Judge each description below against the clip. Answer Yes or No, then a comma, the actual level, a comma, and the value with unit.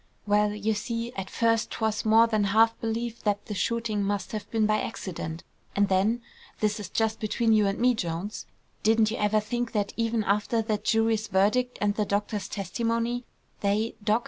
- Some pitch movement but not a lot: No, narrow, 1.8 semitones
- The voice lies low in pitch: No, high, 215 Hz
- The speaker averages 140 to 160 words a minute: No, average, 185 wpm